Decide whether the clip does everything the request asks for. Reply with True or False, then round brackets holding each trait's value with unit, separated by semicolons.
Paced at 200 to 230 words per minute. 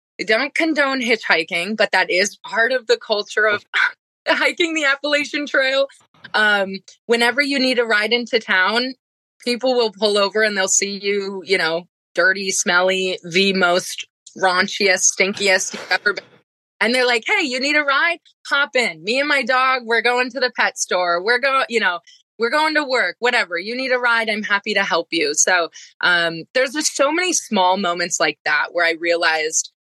False (190 wpm)